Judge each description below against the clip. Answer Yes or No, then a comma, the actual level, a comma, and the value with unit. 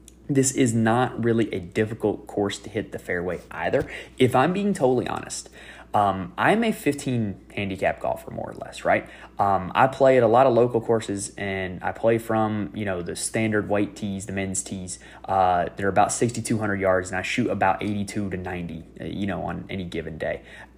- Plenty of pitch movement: No, average, 3.5 semitones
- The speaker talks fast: No, average, 195 wpm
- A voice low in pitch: Yes, low, 105 Hz